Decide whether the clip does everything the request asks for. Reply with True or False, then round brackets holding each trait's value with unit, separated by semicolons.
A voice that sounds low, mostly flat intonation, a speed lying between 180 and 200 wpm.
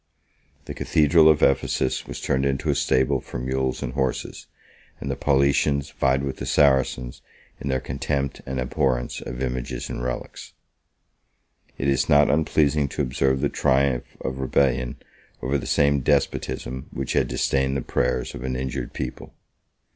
False (65 Hz; 1.5 semitones; 155 wpm)